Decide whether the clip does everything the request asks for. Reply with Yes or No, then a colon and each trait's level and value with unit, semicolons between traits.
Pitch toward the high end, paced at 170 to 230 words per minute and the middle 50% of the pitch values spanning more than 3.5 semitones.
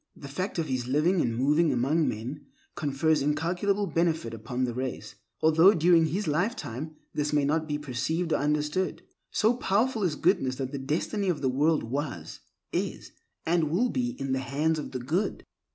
No: medium, 150 Hz; average, 180 wpm; average, 4.4 semitones